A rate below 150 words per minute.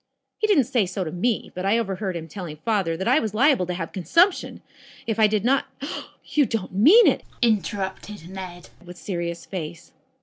No: average, 195 wpm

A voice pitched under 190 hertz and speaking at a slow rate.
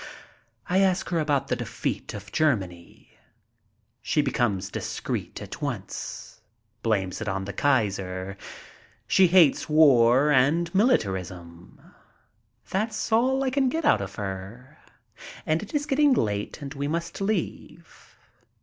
Yes: medium, 140 Hz; slow, 130 wpm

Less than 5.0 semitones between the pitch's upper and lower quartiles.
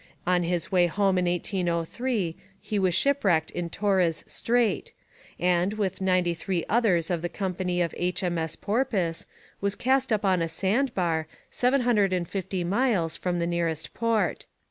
Yes: average, 3.3 semitones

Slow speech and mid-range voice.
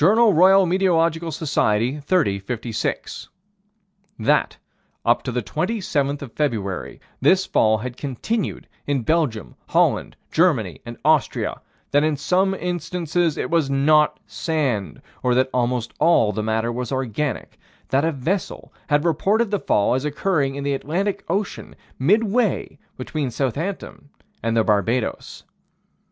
Yes: slow, 130 wpm; medium, 145 Hz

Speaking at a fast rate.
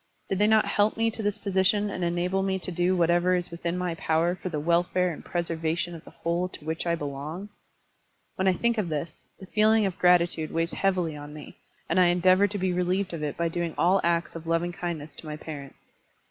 Yes: fast, 230 wpm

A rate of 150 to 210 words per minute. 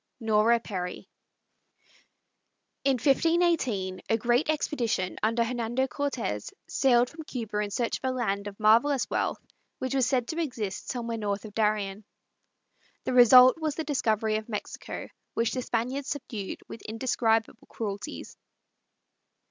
No: slow, 135 wpm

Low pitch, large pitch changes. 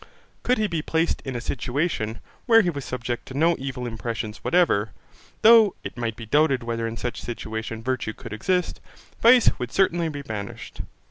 Yes: low, 130 Hz; wide, 6.9 semitones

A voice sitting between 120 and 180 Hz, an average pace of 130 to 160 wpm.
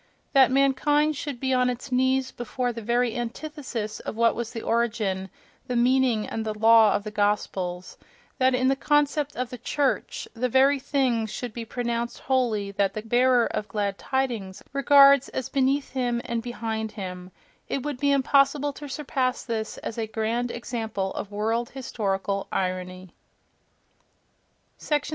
No: high, 240 Hz; average, 155 wpm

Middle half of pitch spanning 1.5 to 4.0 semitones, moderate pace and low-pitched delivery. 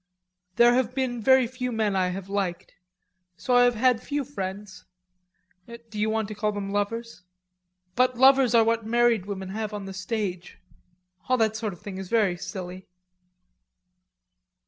No: average, 3.6 semitones; average, 165 wpm; high, 220 Hz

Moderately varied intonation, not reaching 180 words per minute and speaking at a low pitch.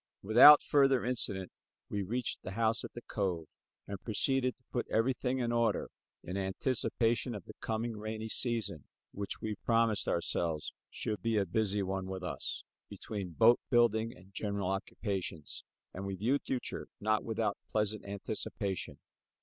Yes: average, 3.4 semitones; average, 155 wpm; low, 110 Hz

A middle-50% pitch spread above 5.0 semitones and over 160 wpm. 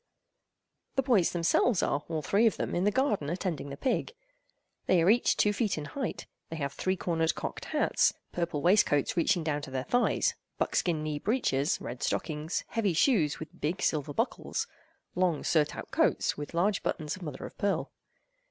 Yes: wide, 5.5 semitones; average, 180 wpm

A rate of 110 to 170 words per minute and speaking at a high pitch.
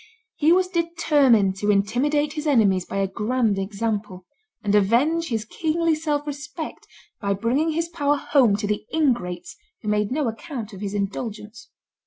Yes: average, 160 wpm; high, 235 Hz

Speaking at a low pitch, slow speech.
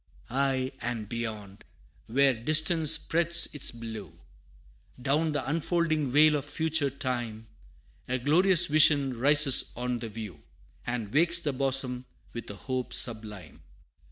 Yes: low, 130 Hz; slow, 130 wpm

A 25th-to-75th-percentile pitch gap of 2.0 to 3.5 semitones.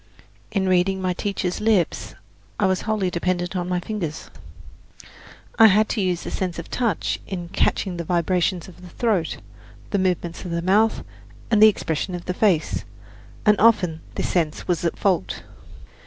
Yes: narrow, 2.6 semitones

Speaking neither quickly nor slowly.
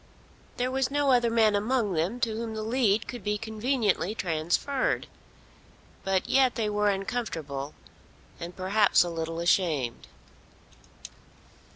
No: slow, 130 wpm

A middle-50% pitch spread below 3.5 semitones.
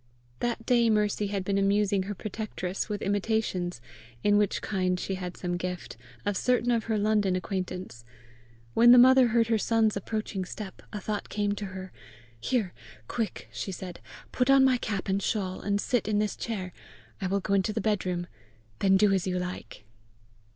Yes: average, 2.8 semitones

